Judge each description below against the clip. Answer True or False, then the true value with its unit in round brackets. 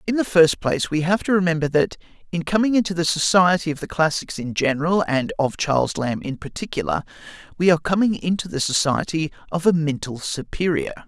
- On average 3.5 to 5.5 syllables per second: False (5.9 syllables/s)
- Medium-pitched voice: True (170 Hz)